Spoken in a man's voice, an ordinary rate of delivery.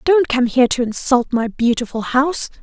No: female; average, 185 wpm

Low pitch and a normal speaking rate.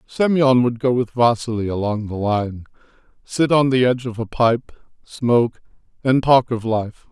Yes: low, 120 Hz; average, 170 wpm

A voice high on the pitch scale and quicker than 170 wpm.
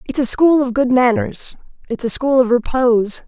Yes: very high, 255 Hz; average, 200 wpm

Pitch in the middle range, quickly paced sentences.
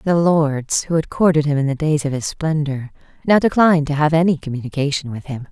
Yes: medium, 150 Hz; fast, 220 wpm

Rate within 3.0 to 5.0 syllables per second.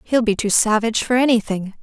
No: 6.0 syllables/s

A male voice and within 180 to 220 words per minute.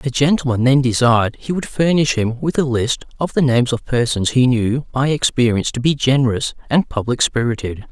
Yes: male; average, 195 wpm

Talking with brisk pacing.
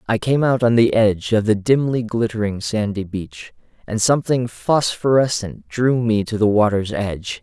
No: average, 170 wpm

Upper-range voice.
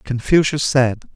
No: low, 135 Hz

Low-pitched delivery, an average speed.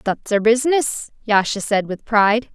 No: high, 220 Hz; average, 165 wpm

